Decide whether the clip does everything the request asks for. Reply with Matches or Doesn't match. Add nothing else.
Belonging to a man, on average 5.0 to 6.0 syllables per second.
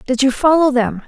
Doesn't match